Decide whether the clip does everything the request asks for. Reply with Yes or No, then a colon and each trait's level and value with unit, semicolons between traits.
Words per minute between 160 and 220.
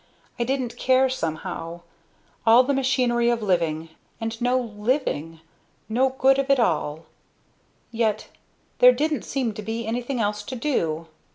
No: average, 145 wpm